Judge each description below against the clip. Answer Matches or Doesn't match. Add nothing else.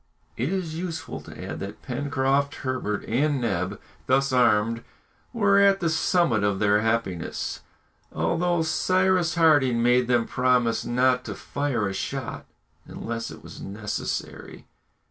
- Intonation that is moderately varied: Doesn't match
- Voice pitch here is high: Doesn't match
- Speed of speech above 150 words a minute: Doesn't match